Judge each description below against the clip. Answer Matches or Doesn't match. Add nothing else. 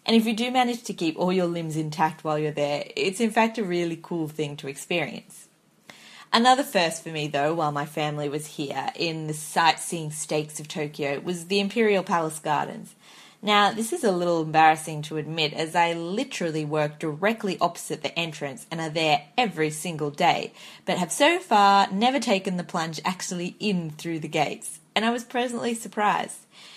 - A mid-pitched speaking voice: Matches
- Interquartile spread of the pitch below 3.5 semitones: Doesn't match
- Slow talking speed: Doesn't match